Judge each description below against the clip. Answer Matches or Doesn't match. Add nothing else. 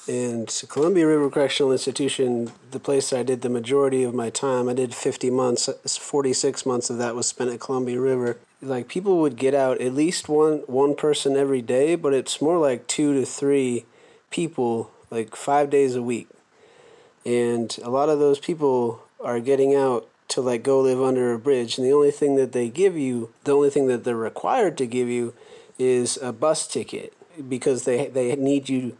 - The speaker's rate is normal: Matches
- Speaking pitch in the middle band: Doesn't match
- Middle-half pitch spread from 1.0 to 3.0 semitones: Matches